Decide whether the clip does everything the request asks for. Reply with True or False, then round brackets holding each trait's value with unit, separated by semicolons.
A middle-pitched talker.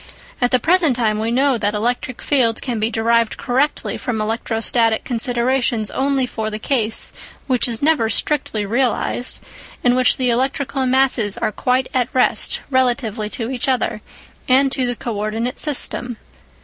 False (245 Hz)